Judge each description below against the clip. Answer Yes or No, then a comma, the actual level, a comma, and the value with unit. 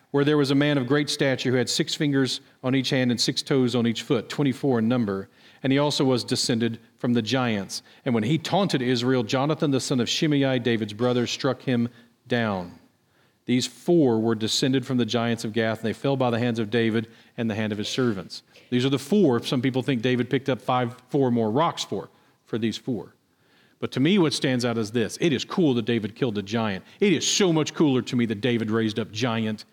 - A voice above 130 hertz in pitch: No, low, 125 Hz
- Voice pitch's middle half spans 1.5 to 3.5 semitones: Yes, average, 3.0 semitones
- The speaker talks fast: Yes, fast, 235 wpm